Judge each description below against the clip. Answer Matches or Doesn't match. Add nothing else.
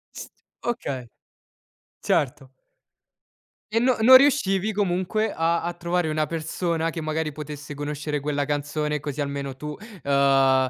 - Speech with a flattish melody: Doesn't match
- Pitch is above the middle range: Doesn't match